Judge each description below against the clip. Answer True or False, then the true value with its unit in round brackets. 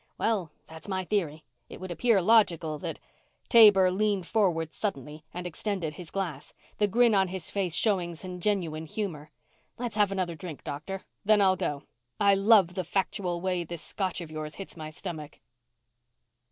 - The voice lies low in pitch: False (185 Hz)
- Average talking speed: True (170 wpm)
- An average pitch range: True (3.8 semitones)